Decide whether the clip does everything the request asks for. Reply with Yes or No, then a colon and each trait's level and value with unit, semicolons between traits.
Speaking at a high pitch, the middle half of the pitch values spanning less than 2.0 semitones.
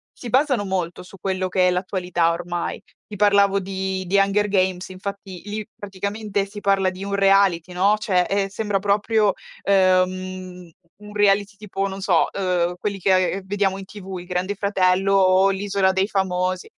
Yes: high, 195 Hz; narrow, 1.5 semitones